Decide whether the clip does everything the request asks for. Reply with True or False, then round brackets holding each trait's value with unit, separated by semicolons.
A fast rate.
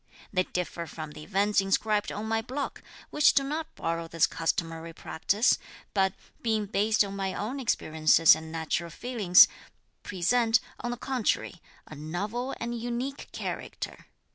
False (145 wpm)